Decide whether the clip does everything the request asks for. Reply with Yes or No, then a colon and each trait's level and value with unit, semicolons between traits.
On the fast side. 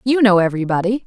Yes: fast, 225 wpm